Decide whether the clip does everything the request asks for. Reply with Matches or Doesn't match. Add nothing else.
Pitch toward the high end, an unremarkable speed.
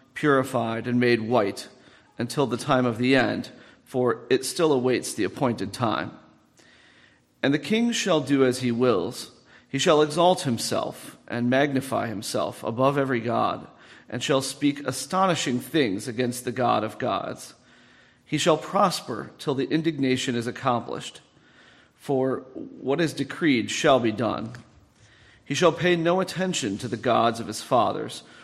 Doesn't match